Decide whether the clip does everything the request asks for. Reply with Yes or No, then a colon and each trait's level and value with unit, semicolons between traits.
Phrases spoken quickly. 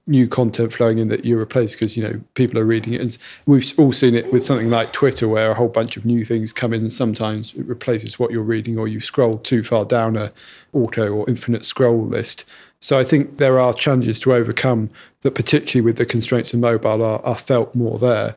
Yes: fast, 230 wpm